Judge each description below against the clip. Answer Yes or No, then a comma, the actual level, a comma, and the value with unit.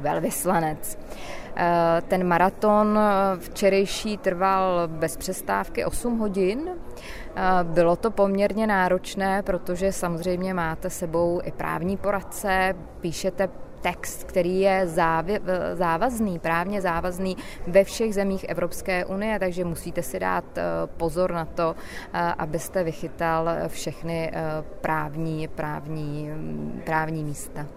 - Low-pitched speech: No, medium, 180 Hz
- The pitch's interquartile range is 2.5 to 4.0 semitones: Yes, average, 2.8 semitones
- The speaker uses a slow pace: Yes, slow, 100 wpm